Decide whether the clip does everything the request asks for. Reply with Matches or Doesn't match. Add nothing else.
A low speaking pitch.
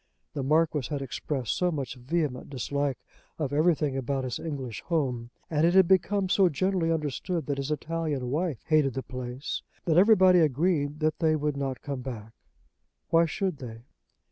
Doesn't match